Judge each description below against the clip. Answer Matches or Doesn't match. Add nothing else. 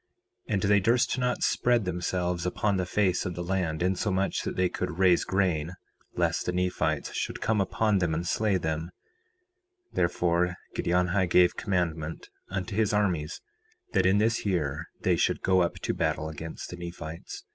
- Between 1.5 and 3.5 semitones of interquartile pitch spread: Matches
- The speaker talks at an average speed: Matches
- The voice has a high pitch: Doesn't match